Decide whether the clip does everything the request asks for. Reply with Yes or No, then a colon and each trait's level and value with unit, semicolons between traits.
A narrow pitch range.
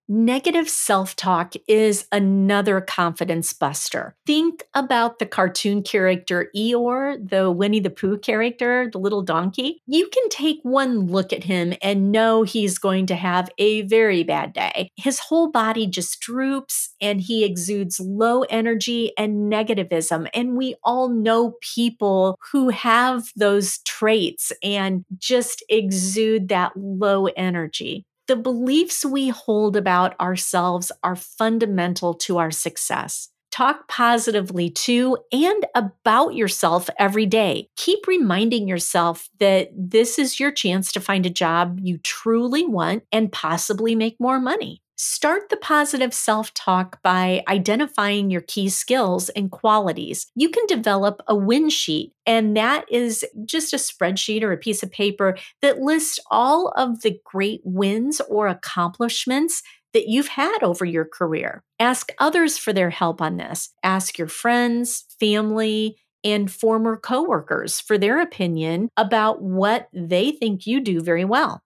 No: average, 4.5 semitones